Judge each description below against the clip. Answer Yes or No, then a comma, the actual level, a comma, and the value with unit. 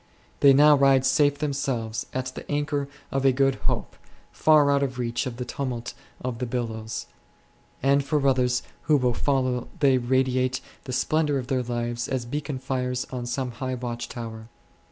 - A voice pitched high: No, low, 130 Hz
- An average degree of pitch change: No, narrow, 2.1 semitones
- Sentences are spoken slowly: No, average, 175 wpm